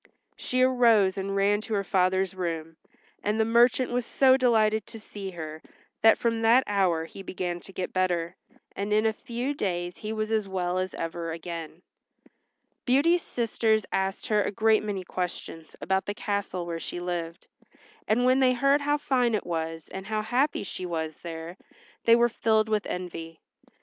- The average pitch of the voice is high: Yes, high, 200 Hz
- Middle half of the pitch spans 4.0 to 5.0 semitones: Yes, average, 4.4 semitones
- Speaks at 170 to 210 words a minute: Yes, average, 180 wpm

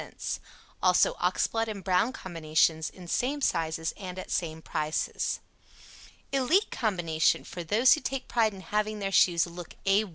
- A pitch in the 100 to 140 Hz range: No, high, 190 Hz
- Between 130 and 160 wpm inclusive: Yes, average, 155 wpm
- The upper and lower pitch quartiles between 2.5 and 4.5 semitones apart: No, average, 5.0 semitones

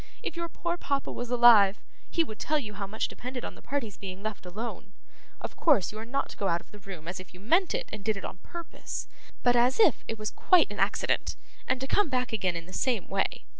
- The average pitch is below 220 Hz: No, high, 225 Hz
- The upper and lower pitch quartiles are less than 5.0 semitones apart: No, wide, 5.5 semitones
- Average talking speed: No, fast, 250 wpm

